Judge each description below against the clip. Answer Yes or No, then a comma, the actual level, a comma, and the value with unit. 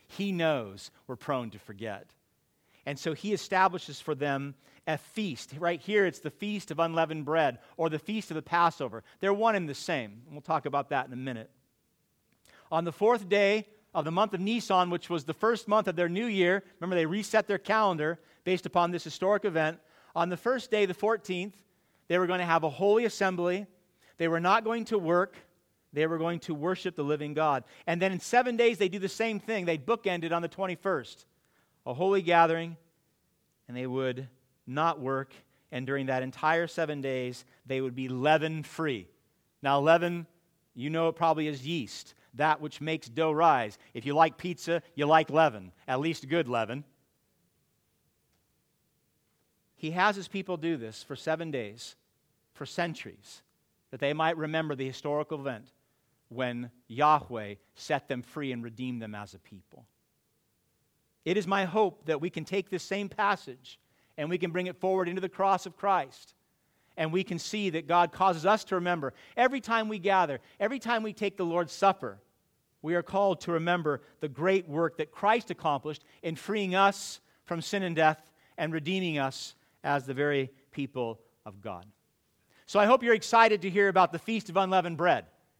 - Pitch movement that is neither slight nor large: Yes, average, 5.0 semitones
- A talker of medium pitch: Yes, medium, 165 Hz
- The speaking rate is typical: Yes, average, 185 wpm